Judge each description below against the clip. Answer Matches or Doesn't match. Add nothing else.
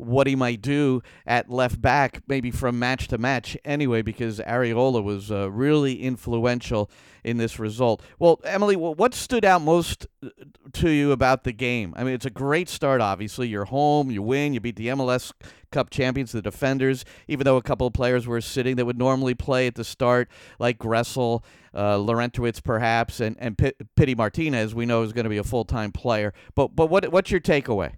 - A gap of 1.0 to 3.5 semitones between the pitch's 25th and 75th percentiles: Matches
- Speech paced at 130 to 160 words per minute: Doesn't match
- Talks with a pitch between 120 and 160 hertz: Matches